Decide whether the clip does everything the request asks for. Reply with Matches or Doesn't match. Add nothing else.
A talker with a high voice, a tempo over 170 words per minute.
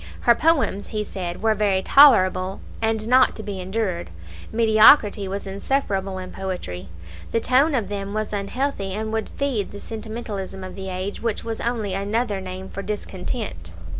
Doesn't match